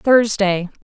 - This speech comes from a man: No, female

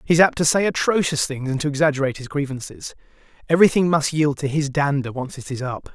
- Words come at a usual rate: No, fast, 220 wpm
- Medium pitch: Yes, medium, 145 Hz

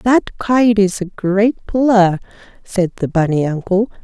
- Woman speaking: Yes, female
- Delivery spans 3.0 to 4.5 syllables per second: Yes, 4.0 syllables/s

